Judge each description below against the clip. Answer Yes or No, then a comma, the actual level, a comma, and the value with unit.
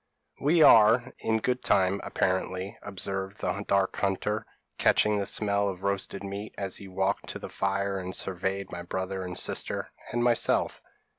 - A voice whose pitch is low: Yes, low, 100 Hz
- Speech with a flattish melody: Yes, narrow, 1.7 semitones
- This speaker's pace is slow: No, average, 170 wpm